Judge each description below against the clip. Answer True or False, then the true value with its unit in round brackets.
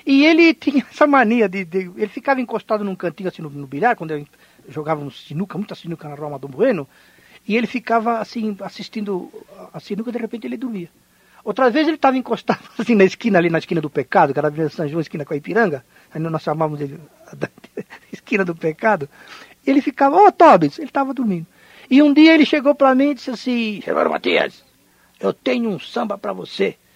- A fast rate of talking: True (220 wpm)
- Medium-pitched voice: False (215 Hz)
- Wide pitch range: True (8.1 semitones)